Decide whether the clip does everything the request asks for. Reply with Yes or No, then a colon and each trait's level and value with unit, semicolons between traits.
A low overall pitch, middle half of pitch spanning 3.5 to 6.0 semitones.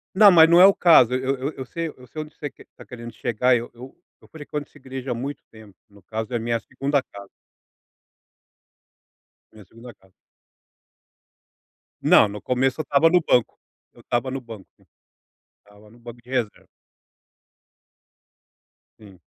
Yes: low, 125 Hz; average, 3.9 semitones